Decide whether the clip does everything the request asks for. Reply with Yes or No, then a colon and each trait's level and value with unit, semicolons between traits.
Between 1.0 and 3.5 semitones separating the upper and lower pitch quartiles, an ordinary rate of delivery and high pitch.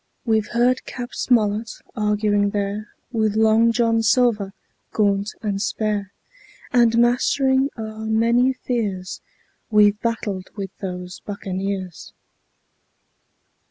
No: narrow, 2.5 semitones; slow, 100 wpm; high, 215 Hz